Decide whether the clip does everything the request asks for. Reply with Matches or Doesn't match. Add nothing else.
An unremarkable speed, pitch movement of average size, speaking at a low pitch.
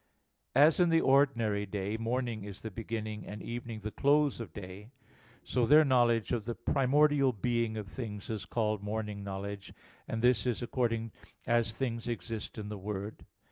Matches